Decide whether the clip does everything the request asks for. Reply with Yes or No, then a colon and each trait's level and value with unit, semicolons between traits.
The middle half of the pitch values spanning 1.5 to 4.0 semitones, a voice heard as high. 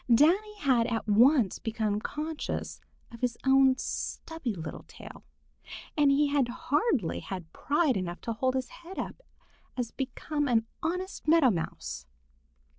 No: average, 5.1 semitones; very high, 260 Hz